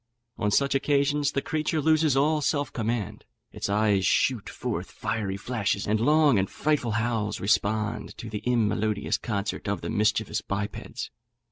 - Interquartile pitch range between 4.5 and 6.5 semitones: Yes, average, 5.1 semitones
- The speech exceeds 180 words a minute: No, average, 150 wpm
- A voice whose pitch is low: Yes, low, 110 Hz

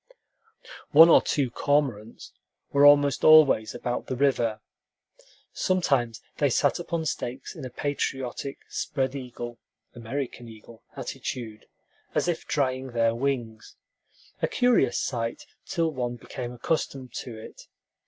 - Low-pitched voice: Yes, low, 130 Hz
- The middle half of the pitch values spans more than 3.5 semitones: No, average, 3.2 semitones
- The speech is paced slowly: Yes, slow, 125 wpm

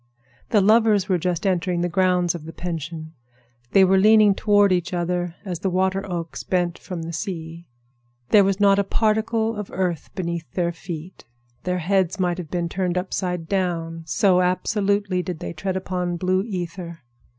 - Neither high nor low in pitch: Yes, medium, 180 Hz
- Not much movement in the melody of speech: Yes, narrow, 2.2 semitones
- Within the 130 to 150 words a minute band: No, average, 175 wpm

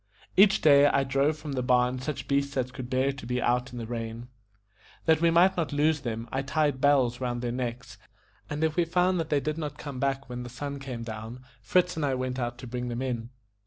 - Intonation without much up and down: No, average, 3.2 semitones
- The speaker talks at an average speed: No, fast, 235 wpm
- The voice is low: Yes, low, 130 Hz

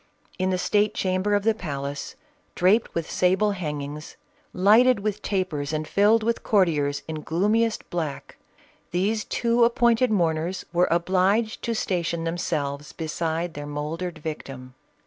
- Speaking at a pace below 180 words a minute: Yes, slow, 135 wpm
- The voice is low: No, medium, 180 Hz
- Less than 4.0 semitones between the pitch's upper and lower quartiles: No, average, 5.1 semitones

